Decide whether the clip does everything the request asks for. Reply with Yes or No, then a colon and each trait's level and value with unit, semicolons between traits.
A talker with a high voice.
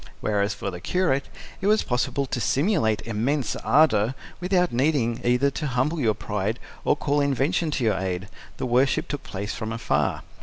No: low, 125 Hz